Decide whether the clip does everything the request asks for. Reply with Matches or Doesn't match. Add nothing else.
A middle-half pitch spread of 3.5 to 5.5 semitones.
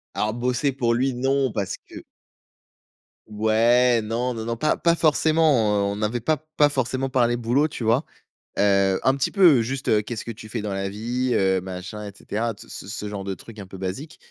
Matches